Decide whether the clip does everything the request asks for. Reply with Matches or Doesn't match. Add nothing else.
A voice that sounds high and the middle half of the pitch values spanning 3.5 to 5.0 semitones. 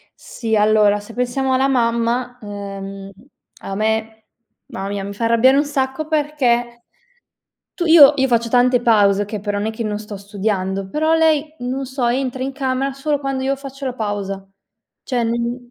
Matches